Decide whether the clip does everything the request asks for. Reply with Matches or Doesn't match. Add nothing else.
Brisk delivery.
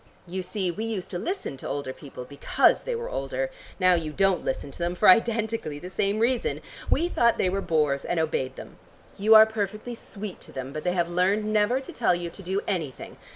Matches